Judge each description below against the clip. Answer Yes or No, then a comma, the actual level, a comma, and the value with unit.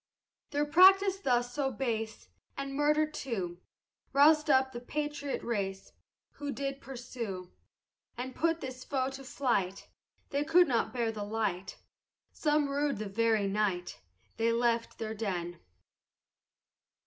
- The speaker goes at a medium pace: No, slow, 130 wpm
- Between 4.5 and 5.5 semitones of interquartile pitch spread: Yes, average, 4.8 semitones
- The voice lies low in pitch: No, very high, 255 Hz